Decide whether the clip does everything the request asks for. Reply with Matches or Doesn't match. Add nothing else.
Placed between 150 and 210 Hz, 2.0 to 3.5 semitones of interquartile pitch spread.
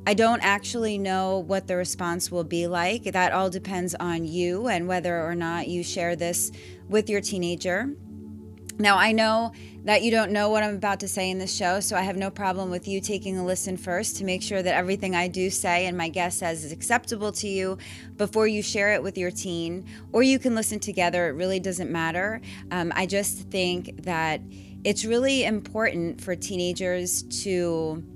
Matches